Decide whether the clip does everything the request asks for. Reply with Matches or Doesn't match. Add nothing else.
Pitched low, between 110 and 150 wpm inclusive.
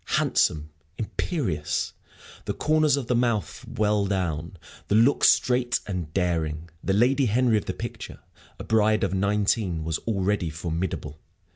Matches